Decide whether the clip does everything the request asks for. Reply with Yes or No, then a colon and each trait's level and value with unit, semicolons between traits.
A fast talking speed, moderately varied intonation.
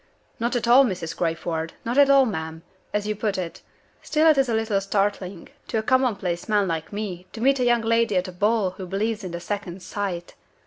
Yes: fast, 220 wpm; average, 4.3 semitones